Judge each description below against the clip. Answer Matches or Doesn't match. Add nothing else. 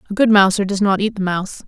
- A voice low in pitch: Doesn't match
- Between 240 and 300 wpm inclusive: Matches